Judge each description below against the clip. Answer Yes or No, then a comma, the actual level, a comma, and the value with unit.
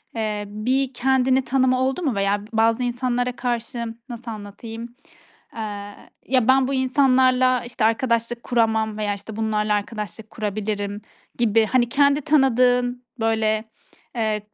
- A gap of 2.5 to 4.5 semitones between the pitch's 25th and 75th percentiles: Yes, average, 2.8 semitones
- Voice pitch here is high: Yes, high, 235 Hz